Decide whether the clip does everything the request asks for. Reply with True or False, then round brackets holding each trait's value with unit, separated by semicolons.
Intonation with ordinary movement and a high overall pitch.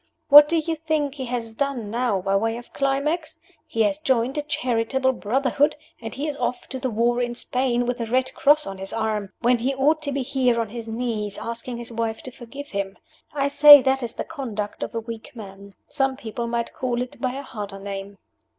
True (3.5 semitones; 245 Hz)